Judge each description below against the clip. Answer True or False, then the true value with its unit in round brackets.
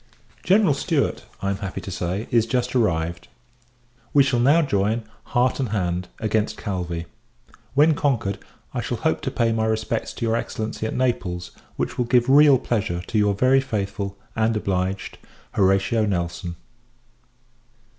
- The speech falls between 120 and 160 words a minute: True (155 wpm)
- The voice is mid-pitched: False (110 Hz)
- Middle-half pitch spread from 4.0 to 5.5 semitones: True (4.4 semitones)